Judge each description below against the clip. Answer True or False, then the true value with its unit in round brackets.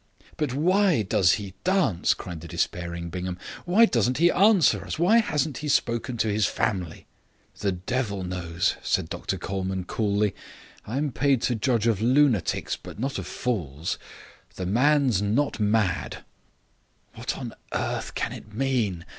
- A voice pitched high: False (110 Hz)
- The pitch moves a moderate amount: False (6.9 semitones)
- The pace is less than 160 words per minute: True (150 wpm)